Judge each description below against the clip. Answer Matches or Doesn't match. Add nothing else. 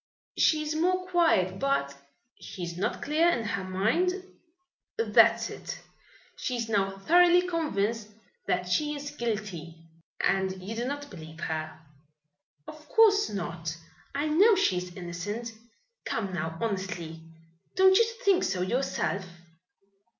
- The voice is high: Matches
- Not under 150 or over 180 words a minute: Doesn't match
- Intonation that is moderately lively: Doesn't match